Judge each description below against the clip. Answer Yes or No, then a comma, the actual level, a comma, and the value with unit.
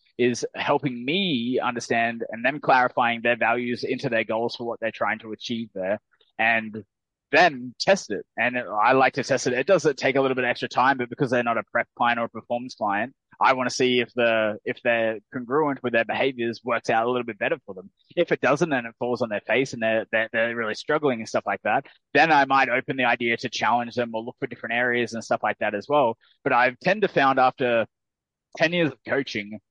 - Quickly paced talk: Yes, fast, 240 wpm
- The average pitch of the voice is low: Yes, low, 120 Hz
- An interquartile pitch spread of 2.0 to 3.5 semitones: Yes, average, 2.7 semitones